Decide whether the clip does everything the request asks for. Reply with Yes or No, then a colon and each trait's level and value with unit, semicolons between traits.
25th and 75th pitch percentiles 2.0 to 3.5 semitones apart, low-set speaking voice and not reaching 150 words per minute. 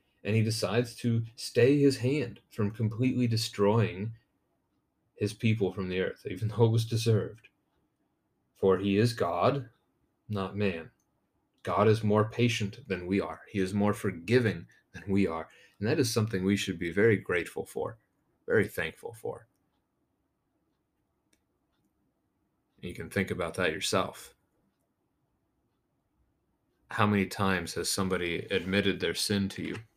Yes: average, 3.2 semitones; low, 105 Hz; average, 140 wpm